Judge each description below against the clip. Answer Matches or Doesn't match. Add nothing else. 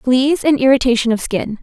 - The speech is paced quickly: Doesn't match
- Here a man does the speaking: Doesn't match